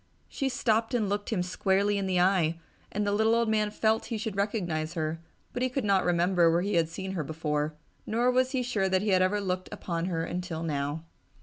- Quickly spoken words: Yes, fast, 225 wpm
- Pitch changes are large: No, average, 4.4 semitones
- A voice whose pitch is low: No, high, 190 Hz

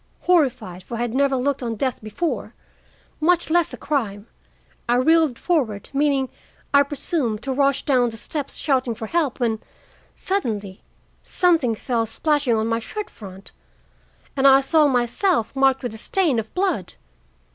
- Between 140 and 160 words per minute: Yes, average, 155 wpm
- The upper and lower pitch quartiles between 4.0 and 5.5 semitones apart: Yes, average, 4.7 semitones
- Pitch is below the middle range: No, very high, 265 Hz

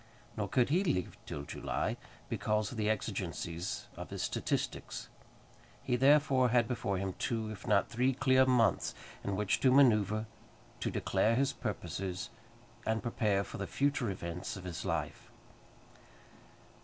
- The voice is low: Yes, low, 110 Hz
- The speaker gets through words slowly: No, average, 145 wpm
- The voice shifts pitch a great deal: No, average, 4.5 semitones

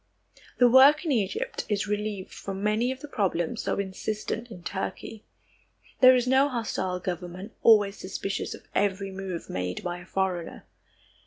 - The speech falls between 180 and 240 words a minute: No, average, 155 wpm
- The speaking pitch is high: Yes, high, 200 Hz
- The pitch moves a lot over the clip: No, average, 3.8 semitones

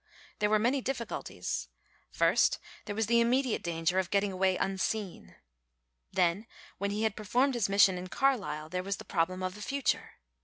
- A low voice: No, high, 200 Hz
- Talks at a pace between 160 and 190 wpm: Yes, average, 170 wpm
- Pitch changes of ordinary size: Yes, average, 4.0 semitones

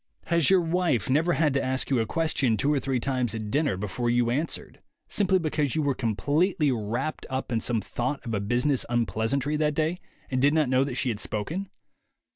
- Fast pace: Yes, fast, 210 wpm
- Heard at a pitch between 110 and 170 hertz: Yes, low, 135 Hz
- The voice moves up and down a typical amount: Yes, average, 4.5 semitones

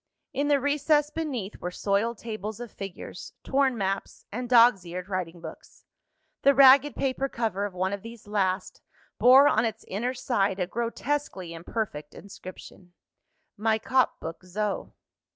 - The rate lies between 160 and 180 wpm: No, average, 150 wpm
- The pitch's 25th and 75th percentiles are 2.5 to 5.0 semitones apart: No, wide, 5.5 semitones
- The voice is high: Yes, high, 220 Hz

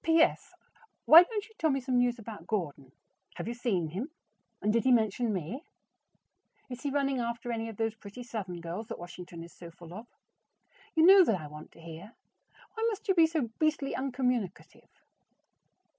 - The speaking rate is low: No, average, 185 wpm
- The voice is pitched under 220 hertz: No, high, 235 Hz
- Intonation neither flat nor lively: No, wide, 6.8 semitones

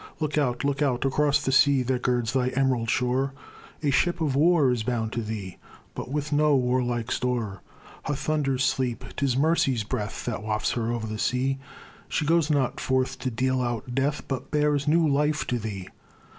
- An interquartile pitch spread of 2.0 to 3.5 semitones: Yes, average, 3.1 semitones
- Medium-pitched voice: No, low, 130 Hz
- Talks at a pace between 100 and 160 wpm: No, average, 190 wpm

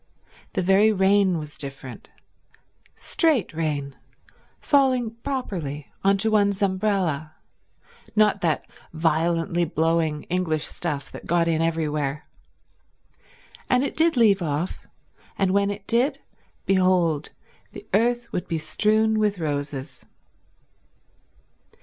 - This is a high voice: No, medium, 180 Hz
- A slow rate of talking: Yes, slow, 110 wpm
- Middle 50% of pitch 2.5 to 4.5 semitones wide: No, average, 5.1 semitones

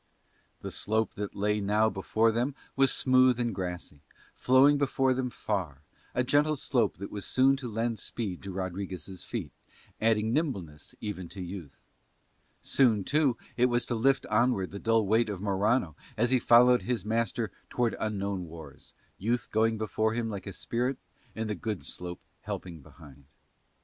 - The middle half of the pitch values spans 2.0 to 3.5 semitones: No, average, 4.1 semitones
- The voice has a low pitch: Yes, low, 110 Hz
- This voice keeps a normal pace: Yes, average, 165 wpm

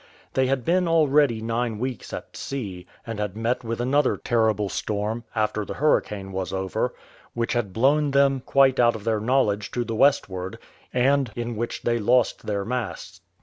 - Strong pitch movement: No, average, 3.9 semitones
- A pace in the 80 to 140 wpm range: No, average, 175 wpm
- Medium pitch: No, low, 115 Hz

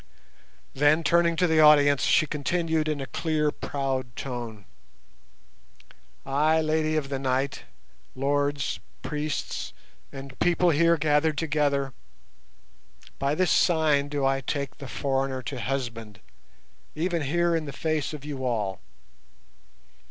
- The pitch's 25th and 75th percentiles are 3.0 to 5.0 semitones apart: No, narrow, 2.5 semitones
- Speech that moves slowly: Yes, slow, 125 wpm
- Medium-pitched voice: Yes, medium, 145 Hz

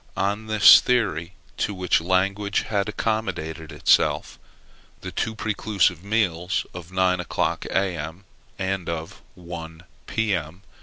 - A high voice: No, very low, 95 Hz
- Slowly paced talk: Yes, slow, 115 wpm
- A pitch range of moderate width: Yes, average, 3.3 semitones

